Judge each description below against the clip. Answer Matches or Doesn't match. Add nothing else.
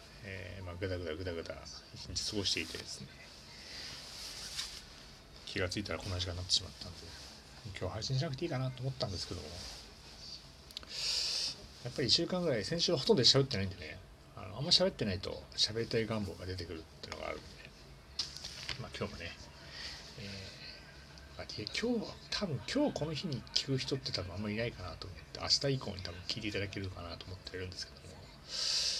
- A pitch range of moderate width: Doesn't match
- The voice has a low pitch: Matches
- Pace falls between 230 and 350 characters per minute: Doesn't match